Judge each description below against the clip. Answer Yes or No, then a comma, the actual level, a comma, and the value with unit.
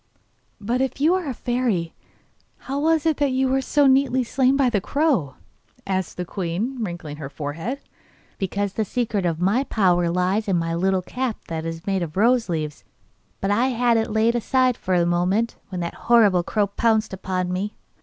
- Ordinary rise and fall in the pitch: No, wide, 6.1 semitones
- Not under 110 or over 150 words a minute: No, average, 190 wpm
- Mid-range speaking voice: No, high, 205 Hz